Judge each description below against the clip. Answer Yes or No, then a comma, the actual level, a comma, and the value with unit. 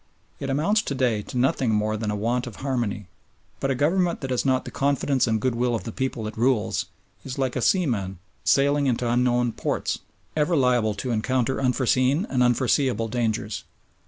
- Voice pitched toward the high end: No, low, 125 Hz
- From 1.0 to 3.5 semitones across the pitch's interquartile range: Yes, average, 3.1 semitones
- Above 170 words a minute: Yes, average, 185 wpm